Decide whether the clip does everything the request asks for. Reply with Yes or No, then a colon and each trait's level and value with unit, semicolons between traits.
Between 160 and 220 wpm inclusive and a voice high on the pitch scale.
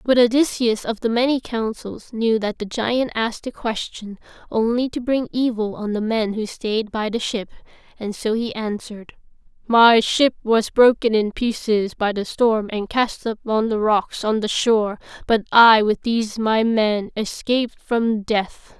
Yes: average, 180 wpm; high, 225 Hz